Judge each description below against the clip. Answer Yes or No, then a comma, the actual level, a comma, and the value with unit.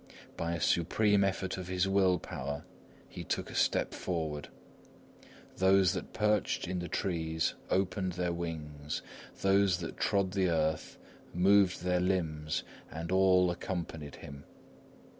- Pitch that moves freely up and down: No, average, 2.8 semitones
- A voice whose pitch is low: Yes, very low, 90 Hz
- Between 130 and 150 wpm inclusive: Yes, slow, 135 wpm